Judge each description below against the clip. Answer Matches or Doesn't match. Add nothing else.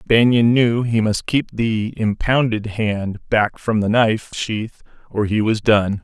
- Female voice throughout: Doesn't match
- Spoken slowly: Doesn't match